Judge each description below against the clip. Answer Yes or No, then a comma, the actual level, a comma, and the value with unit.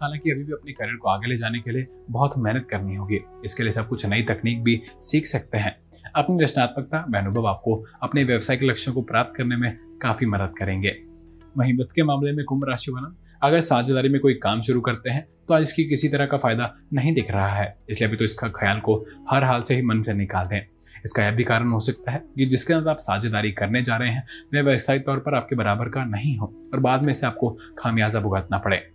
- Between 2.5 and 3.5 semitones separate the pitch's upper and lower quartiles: No, average, 4.2 semitones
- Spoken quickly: Yes, fast, 235 wpm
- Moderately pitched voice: No, low, 120 Hz